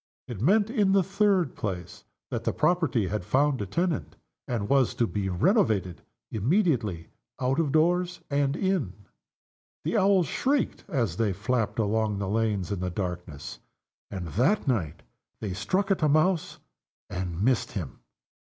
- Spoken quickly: No, average, 150 wpm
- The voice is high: No, low, 120 Hz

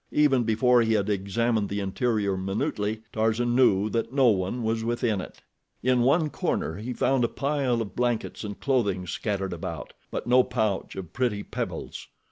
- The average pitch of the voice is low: Yes, low, 115 Hz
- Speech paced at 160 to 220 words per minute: Yes, average, 170 wpm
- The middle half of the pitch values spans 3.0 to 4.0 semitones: Yes, average, 3.4 semitones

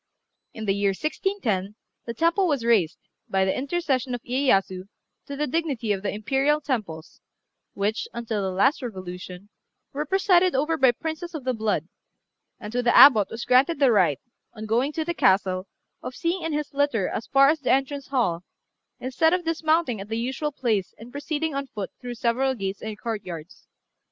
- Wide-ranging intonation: Yes, wide, 6.2 semitones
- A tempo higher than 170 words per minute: Yes, average, 180 wpm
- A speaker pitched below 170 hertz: No, high, 245 Hz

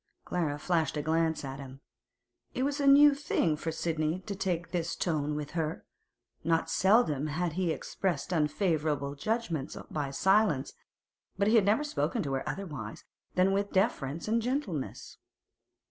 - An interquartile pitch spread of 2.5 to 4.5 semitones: No, average, 5.1 semitones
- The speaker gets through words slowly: No, average, 155 wpm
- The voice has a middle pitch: Yes, medium, 165 Hz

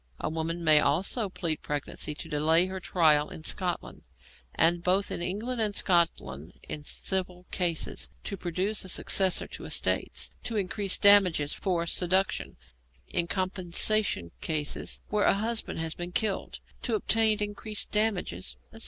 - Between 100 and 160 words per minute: Yes, average, 145 wpm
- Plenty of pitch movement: No, average, 3.9 semitones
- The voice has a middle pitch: Yes, medium, 180 Hz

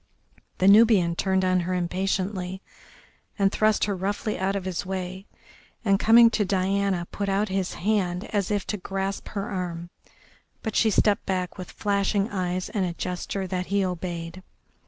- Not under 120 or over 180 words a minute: Yes, average, 165 wpm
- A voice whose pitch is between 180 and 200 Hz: Yes, high, 190 Hz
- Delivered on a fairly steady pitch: Yes, narrow, 1.8 semitones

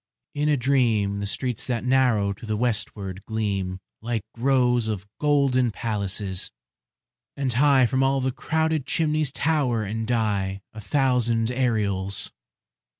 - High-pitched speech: No, low, 120 Hz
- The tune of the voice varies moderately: Yes, average, 4.4 semitones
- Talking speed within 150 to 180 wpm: No, slow, 135 wpm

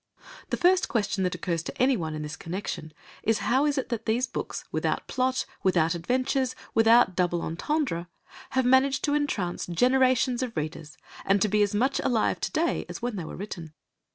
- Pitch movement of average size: No, wide, 6.8 semitones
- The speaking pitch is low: No, high, 225 Hz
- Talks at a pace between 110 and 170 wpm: No, average, 185 wpm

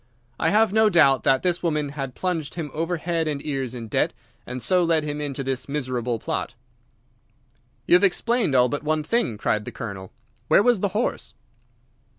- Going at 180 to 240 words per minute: Yes, average, 185 wpm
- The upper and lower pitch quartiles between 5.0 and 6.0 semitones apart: Yes, average, 5.3 semitones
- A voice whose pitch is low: No, medium, 150 Hz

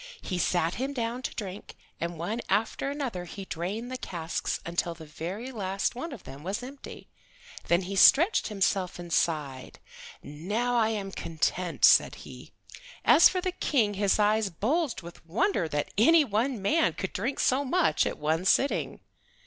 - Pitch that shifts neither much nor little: No, wide, 6.6 semitones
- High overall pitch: Yes, high, 200 Hz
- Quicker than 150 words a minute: Yes, average, 170 wpm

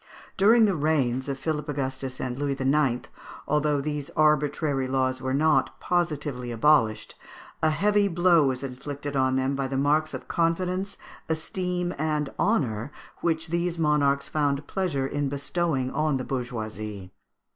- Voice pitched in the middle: Yes, medium, 145 Hz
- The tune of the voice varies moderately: Yes, average, 3.2 semitones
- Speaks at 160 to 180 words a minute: No, average, 145 wpm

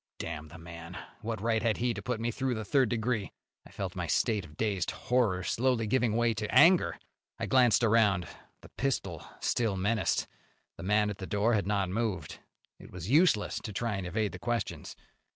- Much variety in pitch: No, average, 3.3 semitones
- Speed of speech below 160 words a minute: No, average, 195 wpm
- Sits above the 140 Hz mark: No, low, 110 Hz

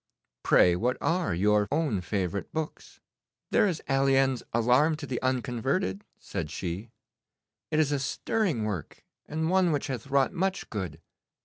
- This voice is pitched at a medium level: No, low, 130 Hz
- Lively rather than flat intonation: Yes, wide, 6.9 semitones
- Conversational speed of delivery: Yes, average, 145 wpm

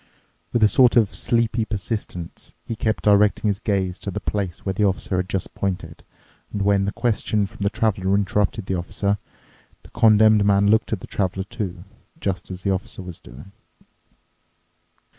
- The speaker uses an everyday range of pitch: No, narrow, 2.2 semitones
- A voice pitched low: Yes, low, 100 Hz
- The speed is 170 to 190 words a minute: Yes, average, 175 wpm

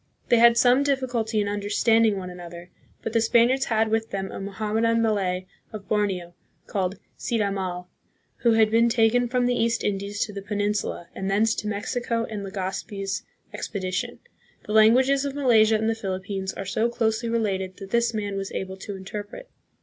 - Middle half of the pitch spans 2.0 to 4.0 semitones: Yes, average, 2.9 semitones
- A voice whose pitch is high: Yes, high, 215 Hz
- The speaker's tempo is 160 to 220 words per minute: Yes, average, 175 wpm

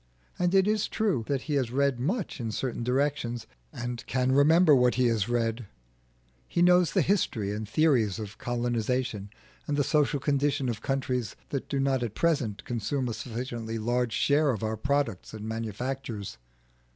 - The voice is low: Yes, low, 125 Hz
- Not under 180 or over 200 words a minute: No, average, 170 wpm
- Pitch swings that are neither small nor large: Yes, average, 4.0 semitones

